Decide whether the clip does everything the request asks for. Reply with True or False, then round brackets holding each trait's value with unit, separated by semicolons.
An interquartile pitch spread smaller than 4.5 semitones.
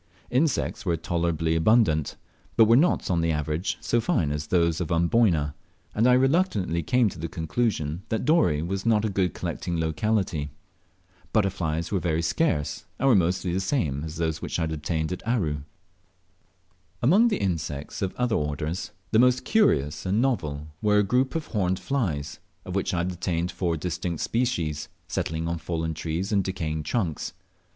False (5.5 semitones)